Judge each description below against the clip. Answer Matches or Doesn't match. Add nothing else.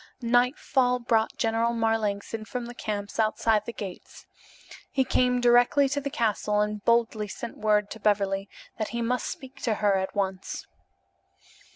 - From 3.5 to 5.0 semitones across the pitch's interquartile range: Doesn't match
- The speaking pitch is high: Matches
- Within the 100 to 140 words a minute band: Doesn't match